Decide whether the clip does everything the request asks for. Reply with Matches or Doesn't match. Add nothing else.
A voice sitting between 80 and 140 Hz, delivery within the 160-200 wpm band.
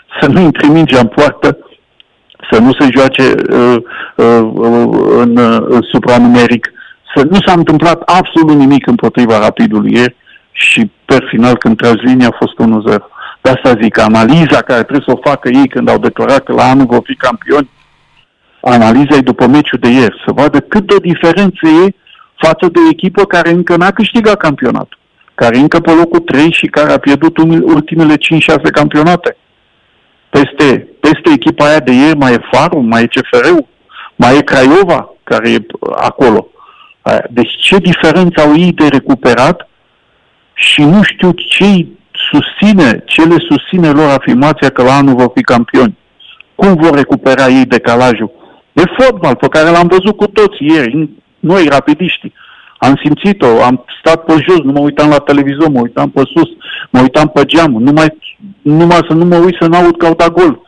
Doesn't match